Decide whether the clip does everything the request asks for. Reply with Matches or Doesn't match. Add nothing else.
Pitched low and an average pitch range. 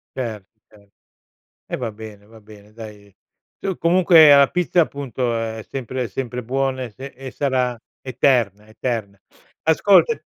Matches